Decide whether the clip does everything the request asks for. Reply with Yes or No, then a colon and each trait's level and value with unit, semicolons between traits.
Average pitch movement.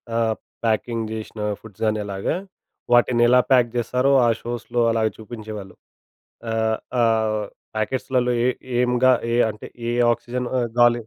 No: narrow, 1.9 semitones